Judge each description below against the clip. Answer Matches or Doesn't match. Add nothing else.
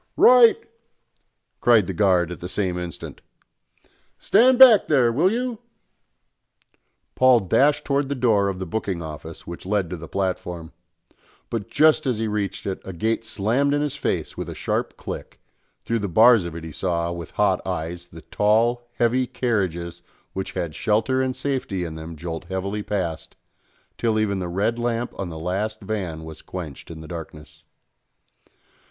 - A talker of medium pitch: Doesn't match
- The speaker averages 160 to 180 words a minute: Matches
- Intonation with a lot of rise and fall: Matches